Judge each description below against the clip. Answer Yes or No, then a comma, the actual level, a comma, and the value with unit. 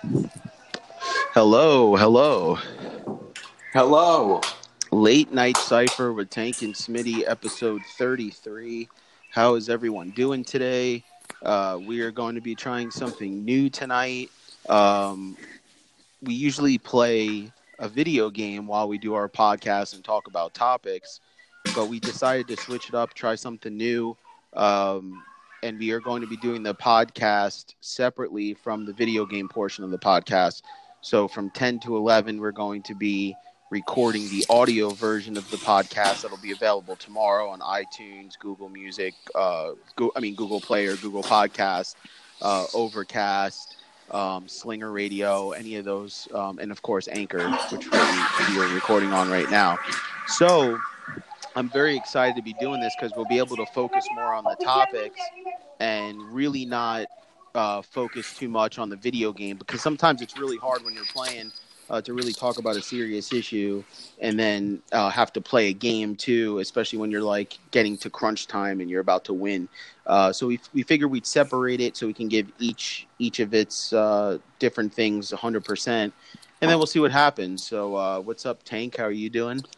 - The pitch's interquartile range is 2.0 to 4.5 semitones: Yes, average, 3.3 semitones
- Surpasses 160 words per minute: Yes, average, 170 wpm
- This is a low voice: Yes, low, 110 Hz